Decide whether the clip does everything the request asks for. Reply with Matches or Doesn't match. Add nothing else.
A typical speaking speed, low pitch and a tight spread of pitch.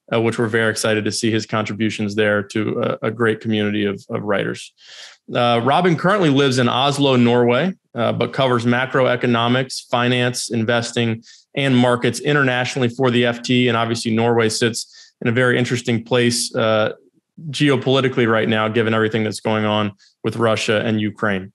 Matches